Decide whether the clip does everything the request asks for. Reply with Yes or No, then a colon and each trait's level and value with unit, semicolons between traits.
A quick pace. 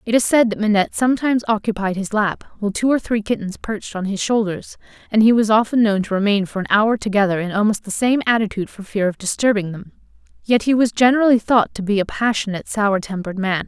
Yes: fast, 225 wpm